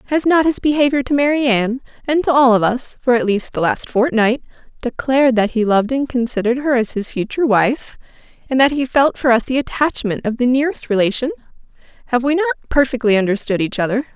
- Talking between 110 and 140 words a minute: No, average, 200 wpm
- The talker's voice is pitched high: Yes, very high, 250 Hz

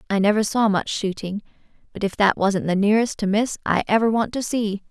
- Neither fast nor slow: No, fast, 220 wpm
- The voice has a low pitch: No, high, 205 Hz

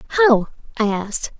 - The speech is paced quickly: No, slow, 130 wpm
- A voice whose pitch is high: Yes, high, 240 Hz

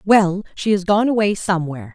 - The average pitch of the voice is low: No, high, 190 Hz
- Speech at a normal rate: Yes, average, 185 wpm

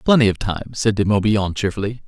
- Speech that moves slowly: No, average, 200 wpm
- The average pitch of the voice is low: Yes, low, 105 Hz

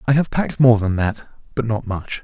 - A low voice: Yes, low, 115 Hz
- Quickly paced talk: Yes, fast, 240 wpm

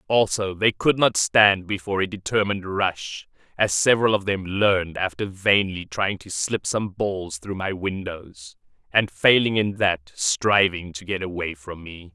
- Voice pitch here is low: Yes, very low, 95 Hz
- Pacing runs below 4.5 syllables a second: Yes, 4.3 syllables/s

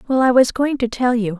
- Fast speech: Yes, fast, 300 wpm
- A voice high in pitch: Yes, high, 245 Hz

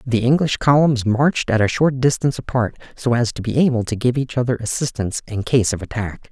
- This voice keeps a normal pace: No, fast, 220 wpm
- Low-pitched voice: Yes, low, 120 Hz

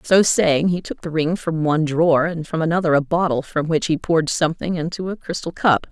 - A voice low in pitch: No, medium, 160 Hz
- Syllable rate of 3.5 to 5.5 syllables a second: No, 5.7 syllables/s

